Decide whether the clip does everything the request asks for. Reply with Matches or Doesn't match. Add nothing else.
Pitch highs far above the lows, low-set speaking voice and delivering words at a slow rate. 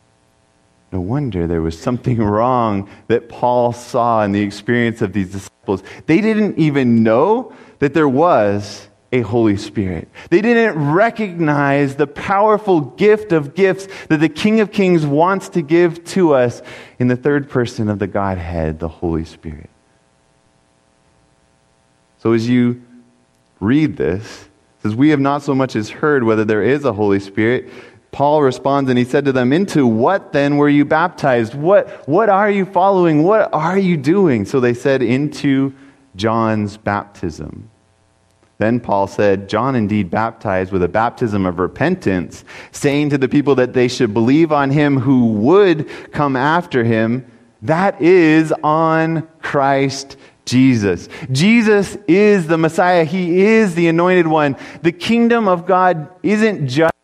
Doesn't match